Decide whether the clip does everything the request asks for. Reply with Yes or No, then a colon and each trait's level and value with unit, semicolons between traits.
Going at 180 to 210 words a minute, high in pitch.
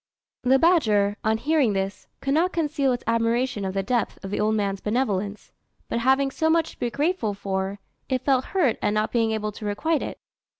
Yes: fast, 205 wpm; high, 230 Hz